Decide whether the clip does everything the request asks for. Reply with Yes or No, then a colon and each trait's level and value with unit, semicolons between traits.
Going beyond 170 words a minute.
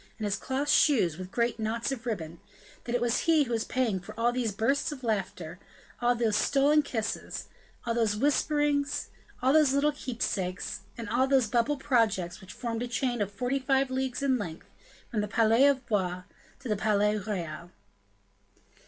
Yes: average, 180 wpm